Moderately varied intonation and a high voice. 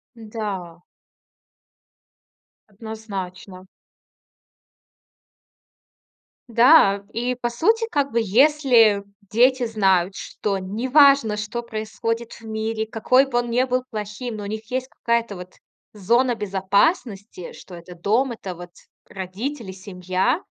Yes: average, 3.8 semitones; high, 220 Hz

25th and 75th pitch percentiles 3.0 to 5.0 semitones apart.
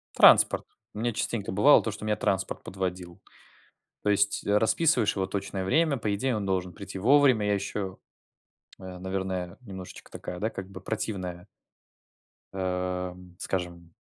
No: narrow, 2.6 semitones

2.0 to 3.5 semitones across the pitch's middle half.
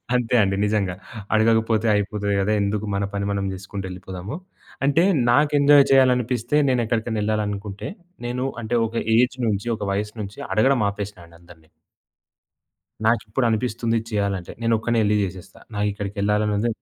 Yes: average, 2.8 semitones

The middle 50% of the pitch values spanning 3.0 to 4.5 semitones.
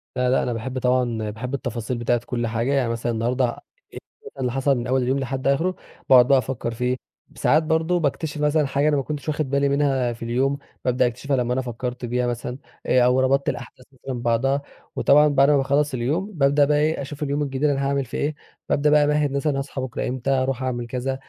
No: narrow, 2.5 semitones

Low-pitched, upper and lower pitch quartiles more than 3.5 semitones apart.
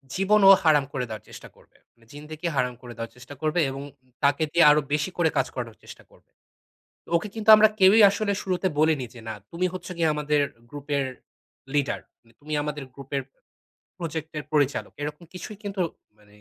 No: medium, 150 Hz; average, 4.3 semitones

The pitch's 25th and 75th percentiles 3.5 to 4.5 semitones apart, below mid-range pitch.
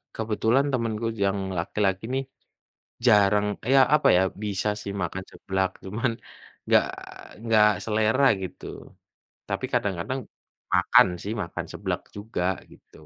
No: average, 2.9 semitones; low, 105 Hz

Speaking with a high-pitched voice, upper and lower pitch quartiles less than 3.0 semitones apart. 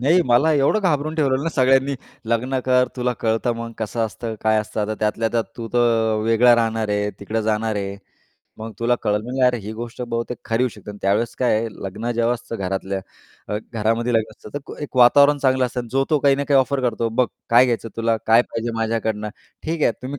No: low, 115 Hz; narrow, 2.6 semitones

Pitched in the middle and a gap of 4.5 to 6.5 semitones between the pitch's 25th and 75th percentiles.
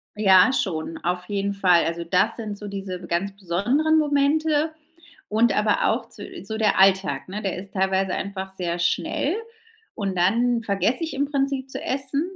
No: high, 200 Hz; wide, 5.6 semitones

